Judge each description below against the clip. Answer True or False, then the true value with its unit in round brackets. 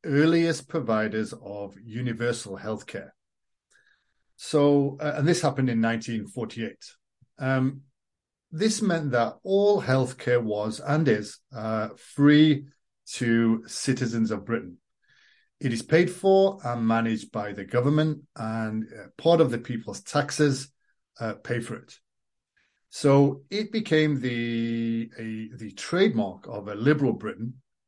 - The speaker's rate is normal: False (125 wpm)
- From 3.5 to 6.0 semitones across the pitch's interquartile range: True (5.0 semitones)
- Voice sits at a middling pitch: False (125 Hz)